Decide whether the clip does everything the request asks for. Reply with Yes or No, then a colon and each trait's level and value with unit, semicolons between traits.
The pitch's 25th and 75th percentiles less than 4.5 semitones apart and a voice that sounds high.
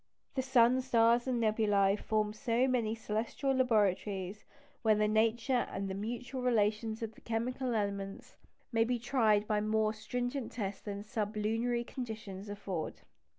Yes: narrow, 2.6 semitones; high, 220 Hz